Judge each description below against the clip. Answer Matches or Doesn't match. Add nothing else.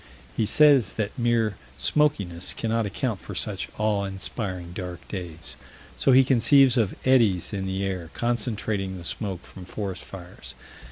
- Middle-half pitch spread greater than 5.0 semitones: Doesn't match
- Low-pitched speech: Matches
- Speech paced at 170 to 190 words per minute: Doesn't match